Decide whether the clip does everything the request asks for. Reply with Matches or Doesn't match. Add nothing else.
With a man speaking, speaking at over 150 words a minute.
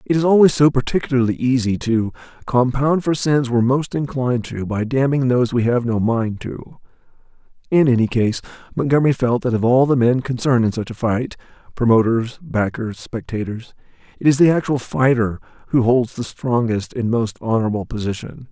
Matches